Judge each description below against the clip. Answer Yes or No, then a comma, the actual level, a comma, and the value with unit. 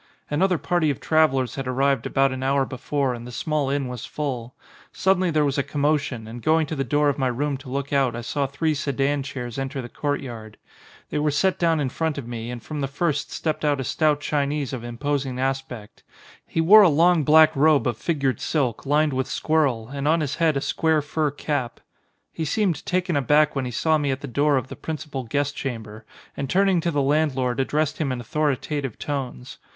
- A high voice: No, medium, 140 Hz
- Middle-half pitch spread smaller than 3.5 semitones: Yes, average, 2.8 semitones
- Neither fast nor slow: No, fast, 220 wpm